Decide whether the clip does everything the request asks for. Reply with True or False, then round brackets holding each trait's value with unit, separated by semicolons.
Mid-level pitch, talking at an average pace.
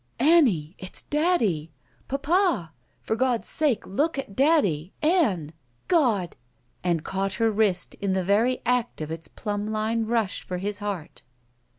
False (215 Hz; 150 wpm)